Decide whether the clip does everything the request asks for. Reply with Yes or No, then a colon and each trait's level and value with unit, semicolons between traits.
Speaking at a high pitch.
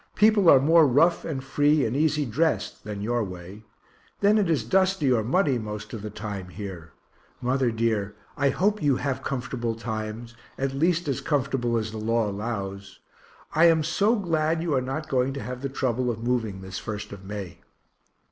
No: low, 125 Hz